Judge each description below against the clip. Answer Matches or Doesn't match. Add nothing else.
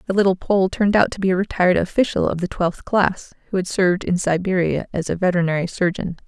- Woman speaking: Matches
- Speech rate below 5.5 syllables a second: Doesn't match